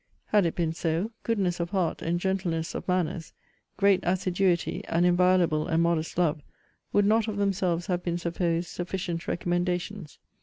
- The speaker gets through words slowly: No, average, 155 wpm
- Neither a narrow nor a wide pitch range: No, narrow, 2.0 semitones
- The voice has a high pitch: No, medium, 175 Hz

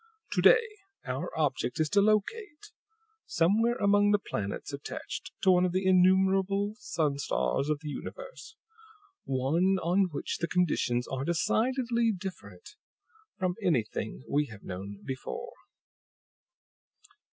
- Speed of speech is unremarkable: No, slow, 125 wpm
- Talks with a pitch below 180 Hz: No, medium, 185 Hz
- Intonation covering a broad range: Yes, wide, 7.0 semitones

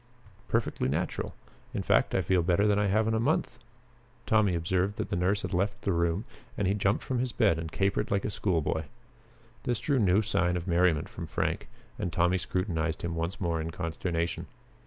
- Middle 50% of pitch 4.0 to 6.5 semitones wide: No, average, 3.3 semitones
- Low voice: Yes, very low, 90 Hz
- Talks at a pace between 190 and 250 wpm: Yes, average, 200 wpm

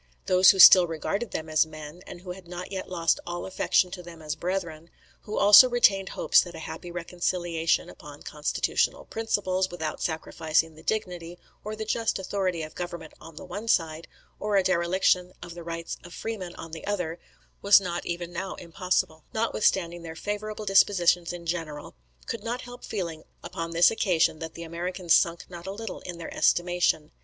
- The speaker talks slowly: No, average, 185 wpm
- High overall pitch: No, medium, 175 Hz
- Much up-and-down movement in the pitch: No, narrow, 2.6 semitones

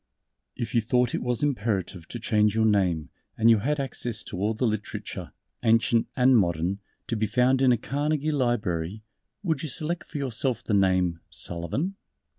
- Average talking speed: Yes, average, 180 wpm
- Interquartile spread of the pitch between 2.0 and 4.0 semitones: No, average, 4.5 semitones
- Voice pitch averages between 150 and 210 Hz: No, low, 115 Hz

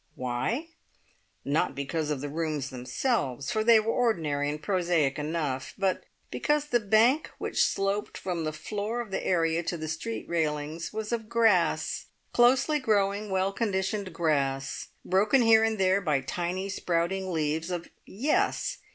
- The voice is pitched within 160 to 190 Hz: Yes, medium, 185 Hz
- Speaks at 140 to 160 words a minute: Yes, average, 150 wpm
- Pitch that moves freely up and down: Yes, wide, 6.0 semitones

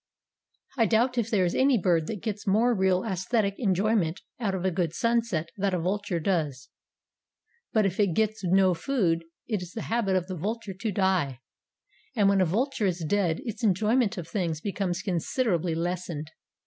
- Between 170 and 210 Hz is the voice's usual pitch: Yes, high, 190 Hz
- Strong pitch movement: No, average, 3.8 semitones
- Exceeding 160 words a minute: Yes, average, 180 wpm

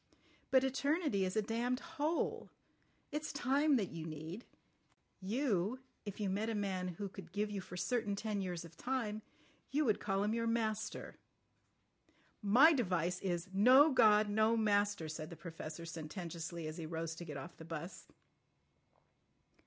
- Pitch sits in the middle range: No, high, 205 Hz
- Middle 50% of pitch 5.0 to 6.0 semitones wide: Yes, wide, 5.4 semitones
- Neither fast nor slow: Yes, average, 155 wpm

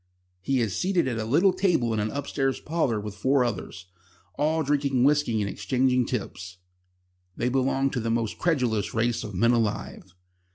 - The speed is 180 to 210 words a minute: No, average, 170 wpm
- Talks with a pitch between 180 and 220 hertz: No, low, 125 Hz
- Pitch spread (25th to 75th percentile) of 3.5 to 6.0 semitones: Yes, average, 4.3 semitones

